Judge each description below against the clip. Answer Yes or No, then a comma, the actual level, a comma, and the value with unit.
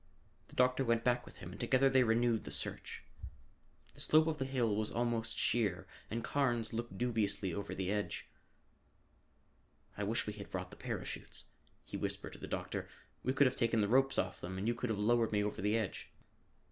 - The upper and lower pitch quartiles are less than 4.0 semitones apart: Yes, average, 3.1 semitones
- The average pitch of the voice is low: Yes, low, 115 Hz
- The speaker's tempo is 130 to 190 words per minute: No, average, 200 wpm